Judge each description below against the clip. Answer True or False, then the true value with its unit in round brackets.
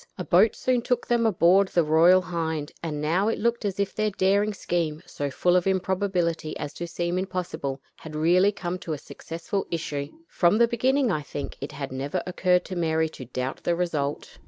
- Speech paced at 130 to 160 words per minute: False (200 wpm)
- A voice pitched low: False (175 Hz)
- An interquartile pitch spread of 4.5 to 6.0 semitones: False (3.8 semitones)